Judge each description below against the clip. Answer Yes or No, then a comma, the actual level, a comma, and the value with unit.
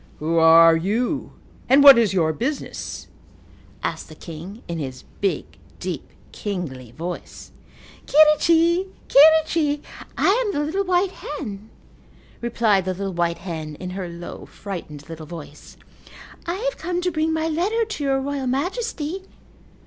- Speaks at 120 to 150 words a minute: Yes, average, 140 wpm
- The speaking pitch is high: Yes, high, 240 Hz